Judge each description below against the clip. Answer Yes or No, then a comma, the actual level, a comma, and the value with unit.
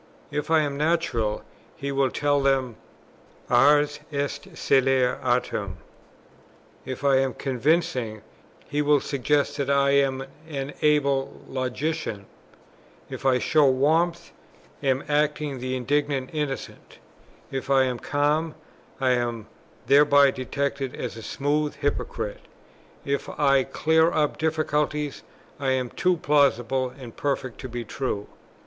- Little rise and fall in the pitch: Yes, narrow, 2.3 semitones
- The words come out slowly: Yes, slow, 130 wpm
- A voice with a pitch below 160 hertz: Yes, medium, 140 Hz